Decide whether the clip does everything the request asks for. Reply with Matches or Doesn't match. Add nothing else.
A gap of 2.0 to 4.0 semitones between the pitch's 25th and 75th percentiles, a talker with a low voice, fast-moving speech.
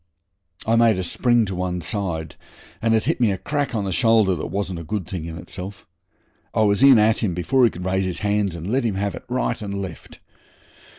Matches